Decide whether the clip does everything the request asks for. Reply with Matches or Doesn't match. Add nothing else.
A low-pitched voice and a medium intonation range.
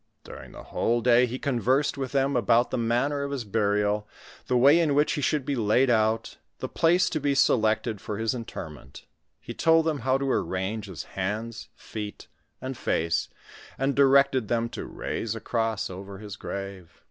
Matches